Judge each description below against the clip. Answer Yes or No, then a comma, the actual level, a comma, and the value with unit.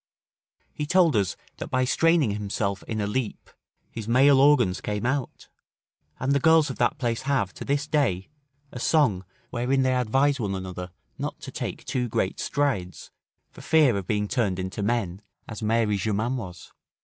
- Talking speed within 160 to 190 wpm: Yes, average, 175 wpm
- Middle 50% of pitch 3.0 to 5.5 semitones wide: Yes, average, 5.2 semitones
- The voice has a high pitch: No, low, 120 Hz